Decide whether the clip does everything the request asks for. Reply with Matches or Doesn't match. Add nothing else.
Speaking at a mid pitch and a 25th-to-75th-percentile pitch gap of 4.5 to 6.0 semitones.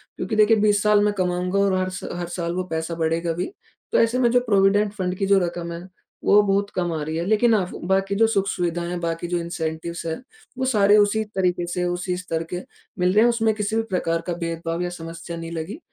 Doesn't match